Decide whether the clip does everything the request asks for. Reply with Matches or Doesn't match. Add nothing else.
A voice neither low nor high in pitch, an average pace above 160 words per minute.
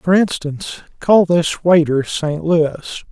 Doesn't match